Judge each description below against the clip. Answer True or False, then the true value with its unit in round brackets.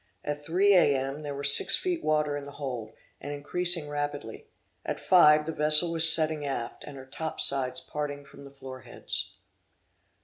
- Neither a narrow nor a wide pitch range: False (2.1 semitones)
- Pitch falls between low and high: True (145 Hz)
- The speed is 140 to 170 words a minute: False (180 wpm)